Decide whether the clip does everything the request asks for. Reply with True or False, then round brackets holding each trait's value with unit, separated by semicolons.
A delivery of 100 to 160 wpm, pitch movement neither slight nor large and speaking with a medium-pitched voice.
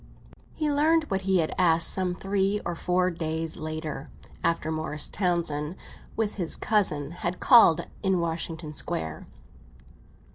True (140 wpm; 3.4 semitones; 170 Hz)